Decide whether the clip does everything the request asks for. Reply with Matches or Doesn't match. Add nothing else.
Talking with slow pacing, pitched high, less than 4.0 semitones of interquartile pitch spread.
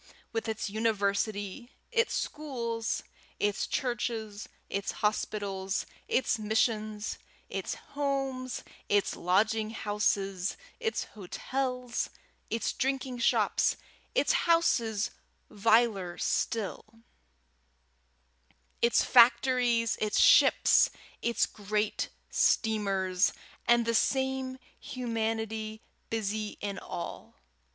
Matches